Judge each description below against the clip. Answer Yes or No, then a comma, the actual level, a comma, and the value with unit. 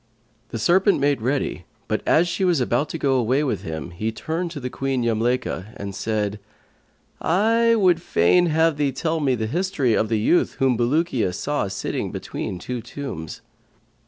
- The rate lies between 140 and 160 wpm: No, average, 170 wpm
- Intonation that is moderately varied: No, wide, 6.8 semitones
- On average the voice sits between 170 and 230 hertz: No, low, 135 Hz